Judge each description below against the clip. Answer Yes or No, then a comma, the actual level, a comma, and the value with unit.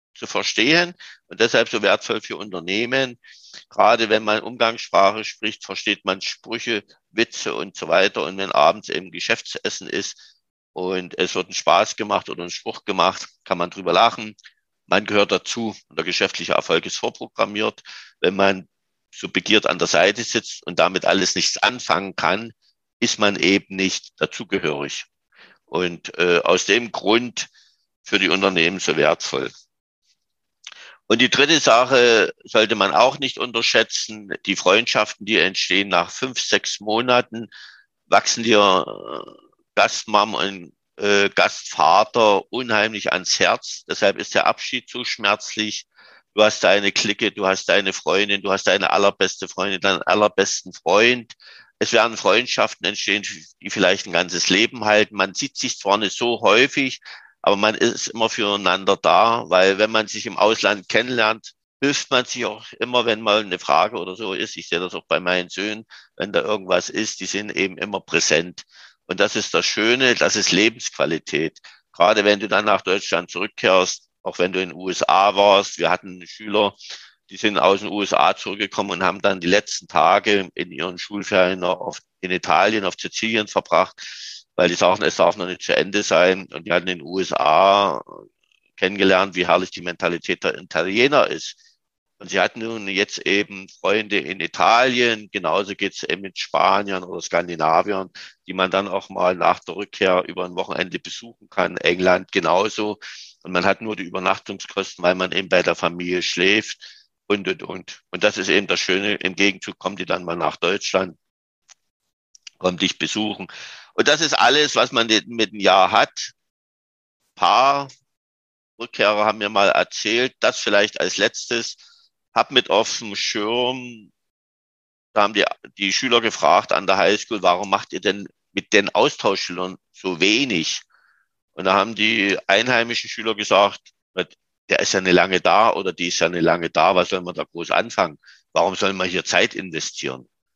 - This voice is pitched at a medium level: No, low, 100 Hz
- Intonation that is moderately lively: Yes, average, 3.1 semitones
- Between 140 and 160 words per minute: No, average, 170 wpm